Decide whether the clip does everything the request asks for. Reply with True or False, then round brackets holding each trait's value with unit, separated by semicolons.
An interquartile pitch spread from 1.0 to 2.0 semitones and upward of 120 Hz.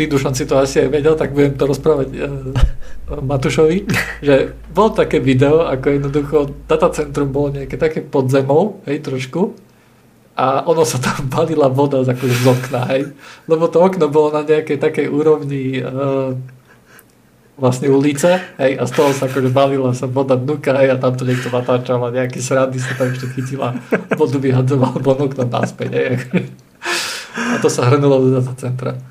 False (2.5 semitones; 140 Hz)